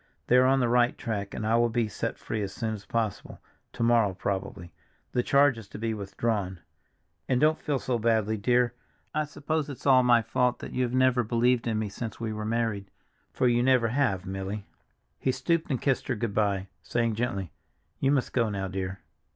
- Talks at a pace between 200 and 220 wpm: Yes, fast, 205 wpm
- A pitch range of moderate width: Yes, average, 3.4 semitones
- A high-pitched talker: No, low, 115 Hz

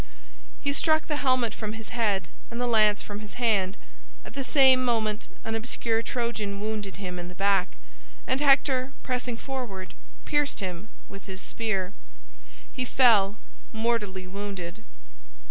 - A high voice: Yes, high, 220 Hz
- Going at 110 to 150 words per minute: Yes, average, 145 wpm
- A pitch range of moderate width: Yes, average, 4.0 semitones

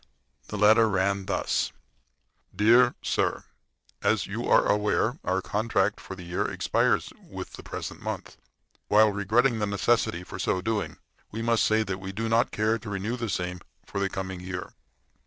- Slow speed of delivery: No, average, 165 wpm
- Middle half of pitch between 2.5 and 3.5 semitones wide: Yes, average, 2.8 semitones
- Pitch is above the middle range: No, low, 105 Hz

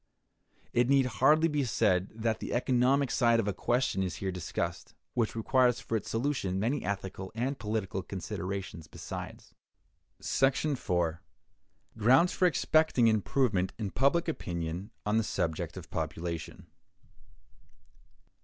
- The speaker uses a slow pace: Yes, slow, 130 wpm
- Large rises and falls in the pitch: Yes, wide, 5.7 semitones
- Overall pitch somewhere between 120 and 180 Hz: No, low, 110 Hz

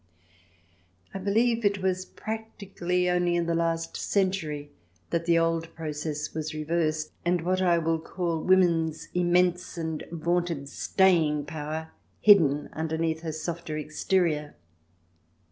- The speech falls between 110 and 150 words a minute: Yes, slow, 135 wpm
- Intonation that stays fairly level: Yes, narrow, 2.3 semitones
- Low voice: No, medium, 165 Hz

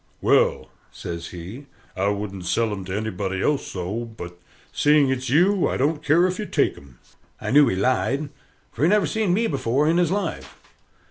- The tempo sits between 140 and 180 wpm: No, average, 190 wpm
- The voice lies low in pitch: Yes, low, 130 Hz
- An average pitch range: No, wide, 8.4 semitones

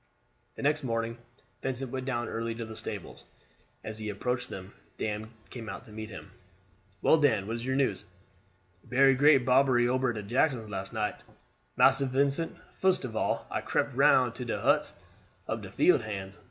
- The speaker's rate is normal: Yes, average, 175 wpm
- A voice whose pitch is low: Yes, low, 120 Hz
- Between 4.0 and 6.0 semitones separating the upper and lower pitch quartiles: No, average, 3.4 semitones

